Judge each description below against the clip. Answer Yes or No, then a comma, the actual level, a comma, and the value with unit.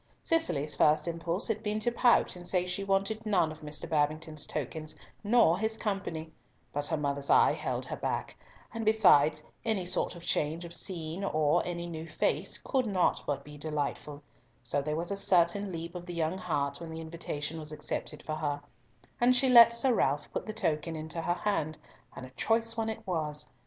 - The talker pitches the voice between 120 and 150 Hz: No, medium, 170 Hz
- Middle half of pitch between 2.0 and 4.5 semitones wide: No, average, 4.9 semitones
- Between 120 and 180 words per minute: No, average, 195 wpm